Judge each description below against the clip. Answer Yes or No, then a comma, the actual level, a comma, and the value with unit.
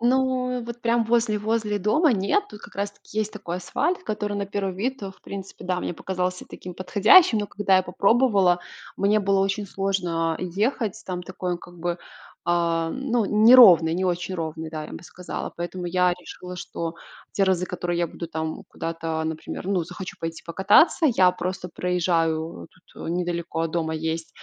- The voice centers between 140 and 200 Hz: Yes, medium, 185 Hz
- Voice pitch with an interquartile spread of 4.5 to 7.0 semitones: No, average, 3.4 semitones